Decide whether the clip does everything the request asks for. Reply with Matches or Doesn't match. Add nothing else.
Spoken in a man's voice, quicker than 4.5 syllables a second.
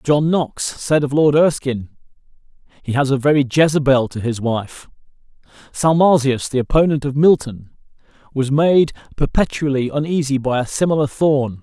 Matches